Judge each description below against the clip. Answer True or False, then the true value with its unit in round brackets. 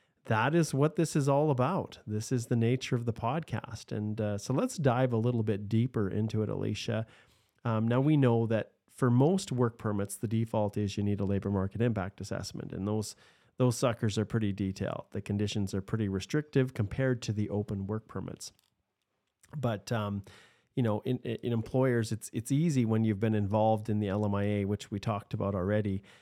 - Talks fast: False (195 wpm)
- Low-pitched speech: True (110 Hz)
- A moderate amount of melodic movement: True (3.4 semitones)